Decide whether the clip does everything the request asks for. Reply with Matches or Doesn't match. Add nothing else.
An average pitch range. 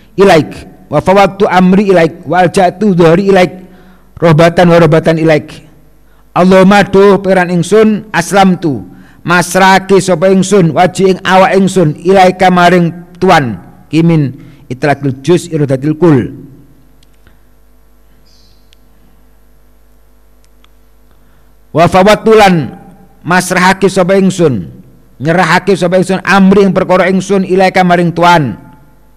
Matches